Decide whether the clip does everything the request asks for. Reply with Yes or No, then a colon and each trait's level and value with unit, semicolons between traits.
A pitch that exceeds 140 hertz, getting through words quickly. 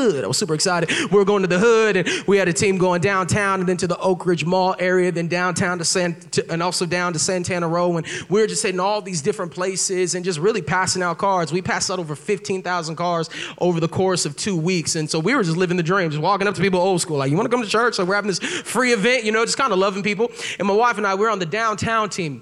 Yes: medium, 185 Hz; fast, 285 wpm